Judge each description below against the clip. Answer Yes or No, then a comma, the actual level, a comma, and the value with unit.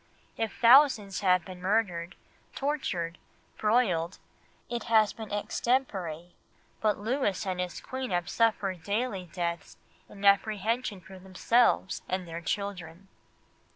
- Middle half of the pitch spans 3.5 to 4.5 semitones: Yes, average, 4.0 semitones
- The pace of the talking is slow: Yes, slow, 120 wpm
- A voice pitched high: Yes, high, 200 Hz